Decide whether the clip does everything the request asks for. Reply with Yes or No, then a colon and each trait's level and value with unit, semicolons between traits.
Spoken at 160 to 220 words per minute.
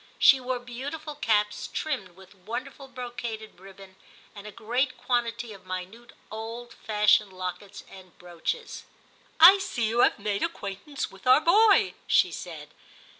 No: average, 150 wpm